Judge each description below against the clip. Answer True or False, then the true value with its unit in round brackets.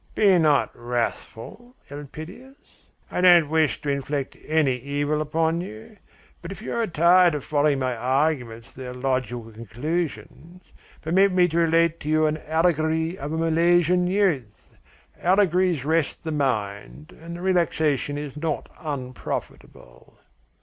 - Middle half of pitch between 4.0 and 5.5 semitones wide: True (4.3 semitones)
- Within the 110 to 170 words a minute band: True (140 wpm)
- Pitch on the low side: False (155 Hz)